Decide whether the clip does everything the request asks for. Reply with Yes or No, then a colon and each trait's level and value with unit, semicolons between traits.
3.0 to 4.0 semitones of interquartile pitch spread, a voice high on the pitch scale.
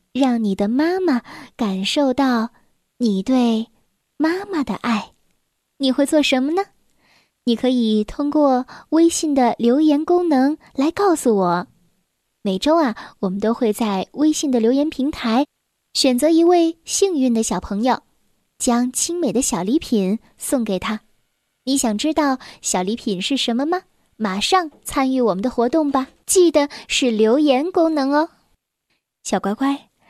No: average, 5.0 semitones; very high, 260 Hz